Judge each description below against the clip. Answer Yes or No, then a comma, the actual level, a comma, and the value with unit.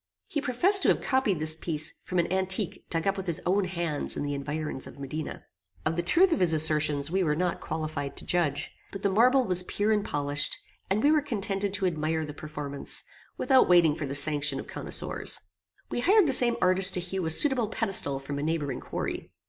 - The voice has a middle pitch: Yes, medium, 175 Hz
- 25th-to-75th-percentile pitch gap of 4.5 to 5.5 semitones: Yes, average, 5.0 semitones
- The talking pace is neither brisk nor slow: No, fast, 215 wpm